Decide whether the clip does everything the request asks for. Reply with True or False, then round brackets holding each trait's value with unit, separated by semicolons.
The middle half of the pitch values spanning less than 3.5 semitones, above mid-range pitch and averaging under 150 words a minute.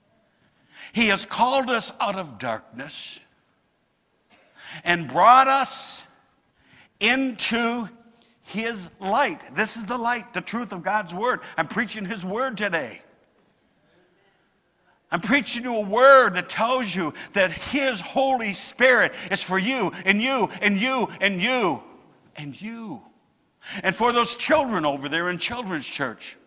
False (4.7 semitones; 225 Hz; 140 wpm)